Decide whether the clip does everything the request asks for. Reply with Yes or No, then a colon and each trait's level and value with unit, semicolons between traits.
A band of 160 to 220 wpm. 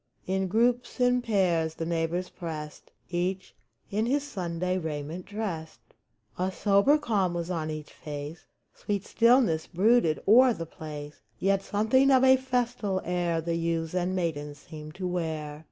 No: average, 150 wpm